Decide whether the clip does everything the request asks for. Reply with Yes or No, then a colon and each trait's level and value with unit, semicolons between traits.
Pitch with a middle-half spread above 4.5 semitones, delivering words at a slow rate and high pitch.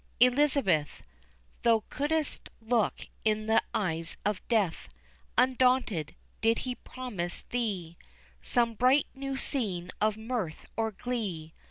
Yes: average, 5.1 semitones; slow, 115 wpm; high, 225 Hz